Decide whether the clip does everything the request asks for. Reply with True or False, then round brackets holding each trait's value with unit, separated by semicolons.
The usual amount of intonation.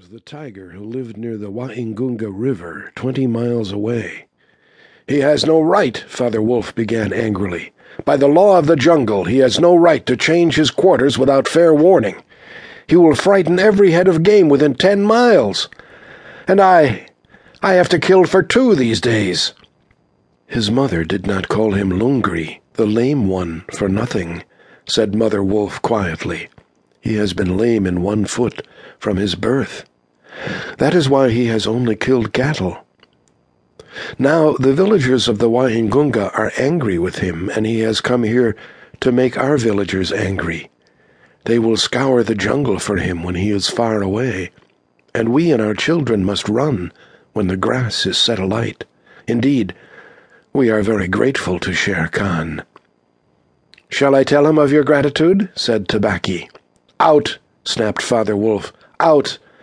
False (5.7 semitones)